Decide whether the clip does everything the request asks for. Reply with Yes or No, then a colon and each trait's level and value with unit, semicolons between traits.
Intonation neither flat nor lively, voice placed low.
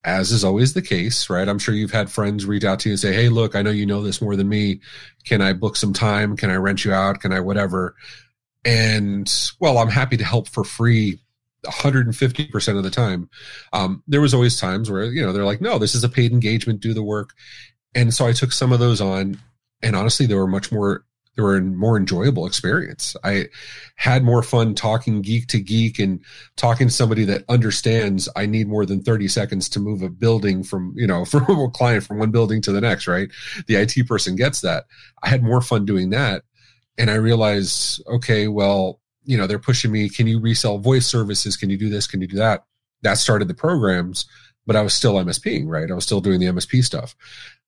Yes: average, 3.1 semitones; low, 110 Hz